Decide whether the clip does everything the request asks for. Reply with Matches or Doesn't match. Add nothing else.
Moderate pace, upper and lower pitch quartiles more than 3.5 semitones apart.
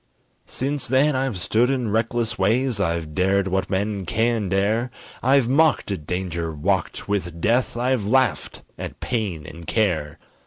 Matches